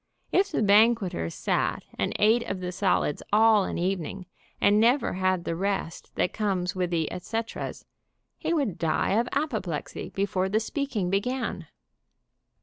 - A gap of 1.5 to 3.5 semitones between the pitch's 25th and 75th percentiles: No, average, 3.9 semitones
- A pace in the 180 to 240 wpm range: No, average, 150 wpm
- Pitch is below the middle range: No, high, 200 Hz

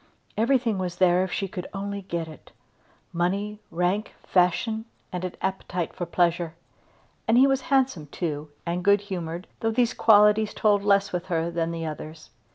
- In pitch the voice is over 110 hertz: Yes, medium, 185 Hz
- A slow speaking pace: No, average, 165 wpm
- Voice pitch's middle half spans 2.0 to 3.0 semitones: No, average, 3.6 semitones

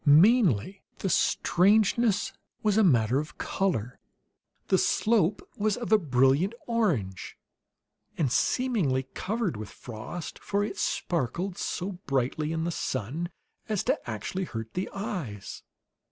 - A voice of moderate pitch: Yes, medium, 175 Hz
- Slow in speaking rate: Yes, slow, 125 wpm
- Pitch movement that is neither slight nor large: No, wide, 7.8 semitones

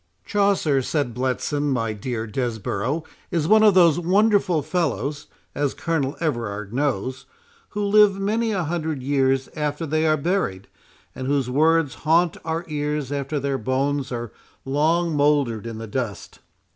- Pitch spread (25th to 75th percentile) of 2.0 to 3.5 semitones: No, average, 4.3 semitones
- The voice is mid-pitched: Yes, medium, 145 Hz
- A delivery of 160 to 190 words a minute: No, average, 145 wpm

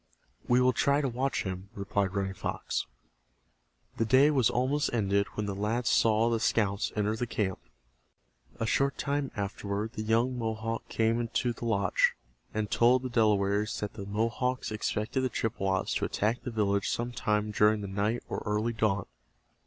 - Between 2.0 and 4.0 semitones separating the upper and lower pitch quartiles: Yes, average, 2.9 semitones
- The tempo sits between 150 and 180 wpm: Yes, average, 170 wpm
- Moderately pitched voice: No, low, 110 Hz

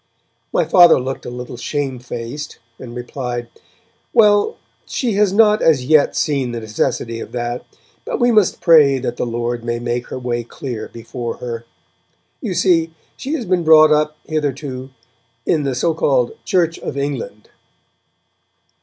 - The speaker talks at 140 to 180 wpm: Yes, average, 155 wpm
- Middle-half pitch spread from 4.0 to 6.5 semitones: Yes, average, 5.2 semitones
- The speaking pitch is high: No, low, 135 Hz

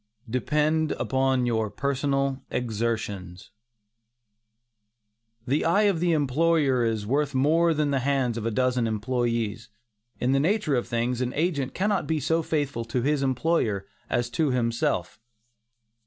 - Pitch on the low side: Yes, low, 130 Hz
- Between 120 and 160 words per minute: Yes, average, 145 wpm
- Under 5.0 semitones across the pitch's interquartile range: Yes, average, 4.4 semitones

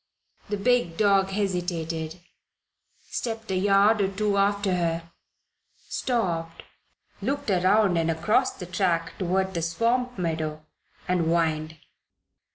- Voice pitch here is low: No, medium, 185 Hz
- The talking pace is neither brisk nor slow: No, slow, 115 wpm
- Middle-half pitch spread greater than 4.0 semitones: No, average, 3.7 semitones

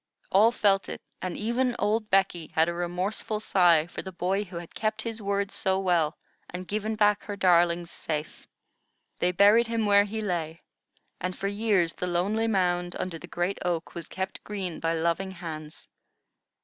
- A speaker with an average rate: Yes, average, 175 wpm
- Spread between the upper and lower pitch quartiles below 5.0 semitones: Yes, average, 3.1 semitones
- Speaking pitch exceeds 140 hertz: Yes, high, 190 Hz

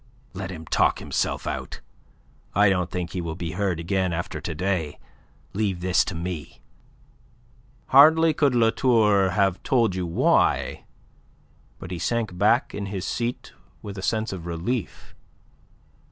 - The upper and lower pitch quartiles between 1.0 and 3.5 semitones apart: No, average, 3.9 semitones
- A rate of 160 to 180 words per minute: No, average, 150 wpm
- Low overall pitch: Yes, very low, 95 Hz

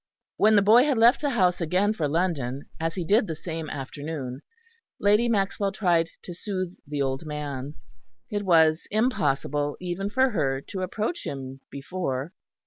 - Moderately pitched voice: Yes, medium, 175 Hz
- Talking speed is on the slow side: No, average, 160 wpm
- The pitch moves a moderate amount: No, wide, 5.9 semitones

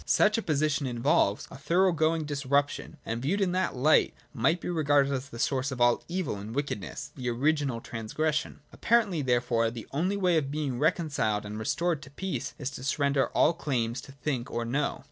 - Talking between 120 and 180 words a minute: No, average, 190 wpm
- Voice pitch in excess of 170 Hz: No, medium, 140 Hz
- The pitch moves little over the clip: No, average, 4.5 semitones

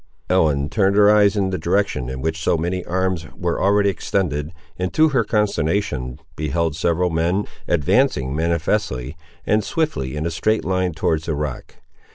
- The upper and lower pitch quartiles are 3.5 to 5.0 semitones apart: Yes, average, 4.4 semitones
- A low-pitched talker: Yes, very low, 85 Hz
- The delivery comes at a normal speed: Yes, average, 165 wpm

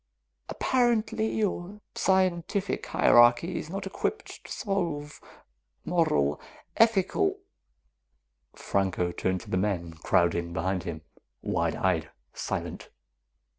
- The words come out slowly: Yes, slow, 100 wpm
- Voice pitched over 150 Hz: No, medium, 145 Hz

